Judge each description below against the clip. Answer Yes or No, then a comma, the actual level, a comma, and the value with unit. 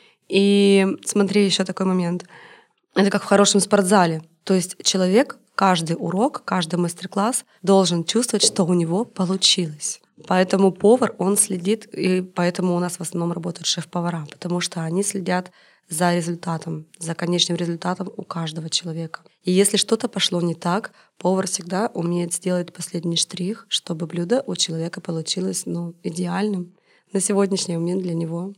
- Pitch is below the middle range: No, medium, 185 Hz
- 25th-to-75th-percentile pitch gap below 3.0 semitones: Yes, narrow, 2.4 semitones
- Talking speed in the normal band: Yes, average, 150 wpm